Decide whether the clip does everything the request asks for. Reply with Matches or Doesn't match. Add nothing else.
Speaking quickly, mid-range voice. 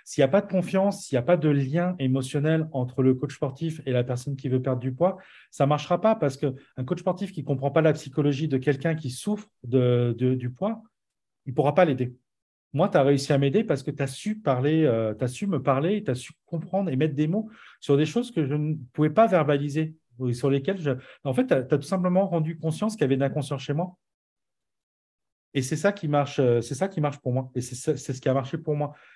Matches